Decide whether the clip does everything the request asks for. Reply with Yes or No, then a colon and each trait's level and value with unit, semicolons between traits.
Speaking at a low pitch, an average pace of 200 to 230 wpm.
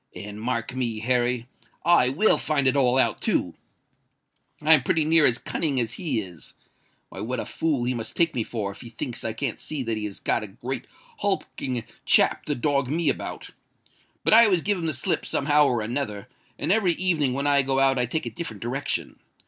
Yes: low, 130 Hz; fast, 205 wpm